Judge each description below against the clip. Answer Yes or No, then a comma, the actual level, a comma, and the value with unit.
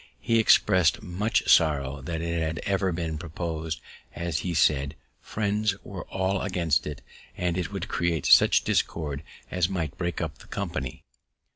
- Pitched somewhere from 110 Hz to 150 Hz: No, very low, 85 Hz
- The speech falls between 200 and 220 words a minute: No, average, 155 wpm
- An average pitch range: Yes, average, 3.0 semitones